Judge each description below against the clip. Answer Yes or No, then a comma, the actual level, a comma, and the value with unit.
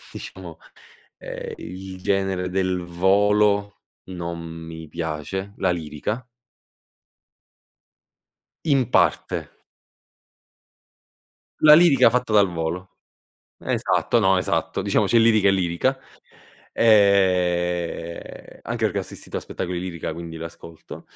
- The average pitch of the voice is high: No, very low, 95 Hz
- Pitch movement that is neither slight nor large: Yes, average, 3.4 semitones